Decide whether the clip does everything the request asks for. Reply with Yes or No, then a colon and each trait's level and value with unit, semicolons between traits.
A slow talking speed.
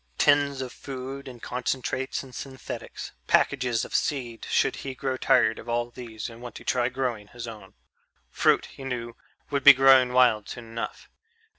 No: average, 170 wpm